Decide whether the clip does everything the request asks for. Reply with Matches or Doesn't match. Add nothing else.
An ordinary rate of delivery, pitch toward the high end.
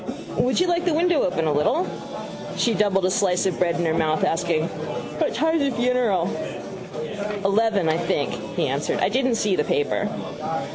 Matches